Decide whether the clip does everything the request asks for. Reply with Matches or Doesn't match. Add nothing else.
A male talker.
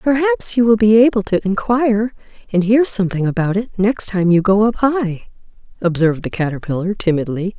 Doesn't match